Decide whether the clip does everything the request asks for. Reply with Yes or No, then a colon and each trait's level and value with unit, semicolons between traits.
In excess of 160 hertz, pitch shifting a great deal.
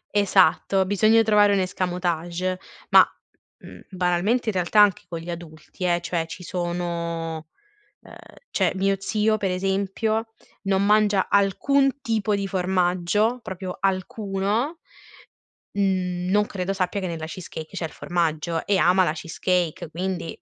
No: medium, 185 Hz; average, 2.7 semitones